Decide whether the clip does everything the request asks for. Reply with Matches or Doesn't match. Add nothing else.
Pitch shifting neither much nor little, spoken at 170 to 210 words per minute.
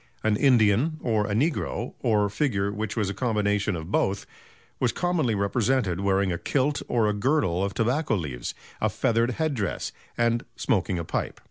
Matches